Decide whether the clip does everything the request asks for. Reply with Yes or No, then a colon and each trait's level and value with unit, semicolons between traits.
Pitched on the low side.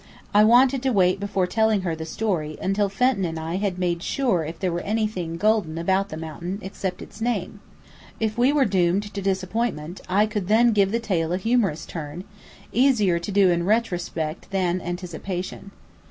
No: high, 190 Hz